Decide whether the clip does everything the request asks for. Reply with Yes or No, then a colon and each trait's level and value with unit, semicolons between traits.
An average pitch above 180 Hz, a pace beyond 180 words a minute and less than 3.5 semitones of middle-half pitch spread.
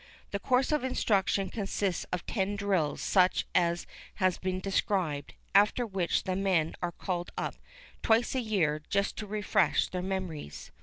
No: high, 190 Hz; average, 155 wpm; narrow, 2.6 semitones